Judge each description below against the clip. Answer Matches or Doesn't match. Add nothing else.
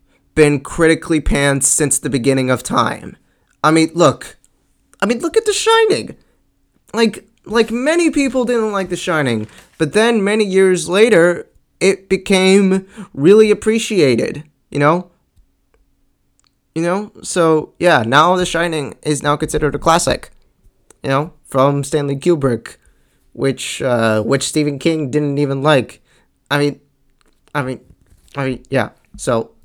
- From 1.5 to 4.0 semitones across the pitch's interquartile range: Doesn't match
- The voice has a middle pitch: Matches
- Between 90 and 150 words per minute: Matches